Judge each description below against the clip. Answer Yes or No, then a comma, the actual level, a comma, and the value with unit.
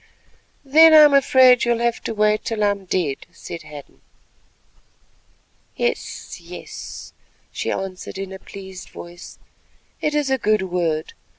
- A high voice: Yes, high, 210 Hz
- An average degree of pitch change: No, wide, 6.0 semitones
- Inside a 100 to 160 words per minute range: Yes, average, 150 wpm